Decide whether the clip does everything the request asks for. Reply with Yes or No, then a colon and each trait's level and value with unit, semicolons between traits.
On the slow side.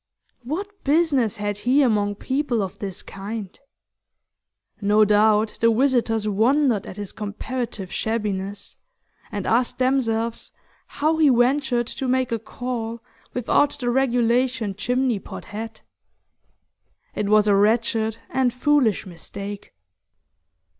Yes: slow, 120 wpm